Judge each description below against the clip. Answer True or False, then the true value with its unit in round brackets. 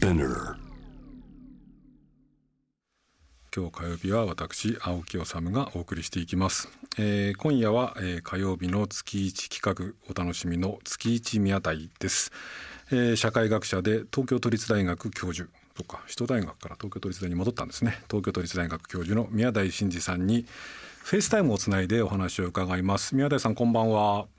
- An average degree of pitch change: True (4.3 semitones)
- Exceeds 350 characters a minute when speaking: False (300 characters per minute)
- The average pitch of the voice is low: True (100 Hz)